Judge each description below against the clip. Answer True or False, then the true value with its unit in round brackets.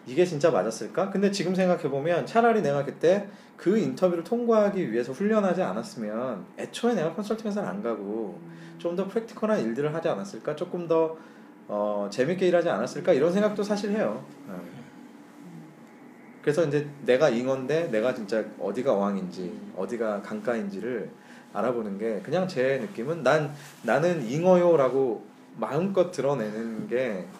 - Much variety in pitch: True (6.9 semitones)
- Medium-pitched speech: True (170 Hz)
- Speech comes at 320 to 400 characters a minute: True (335 characters per minute)